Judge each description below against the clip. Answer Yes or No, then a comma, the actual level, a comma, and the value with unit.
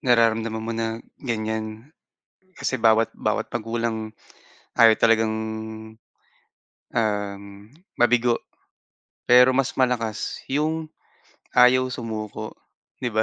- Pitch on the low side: Yes, low, 115 Hz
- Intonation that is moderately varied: No, narrow, 2.1 semitones